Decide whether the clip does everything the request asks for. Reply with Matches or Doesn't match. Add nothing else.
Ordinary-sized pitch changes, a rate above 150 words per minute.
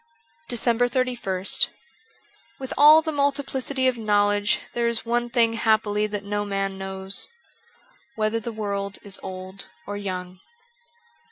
Doesn't match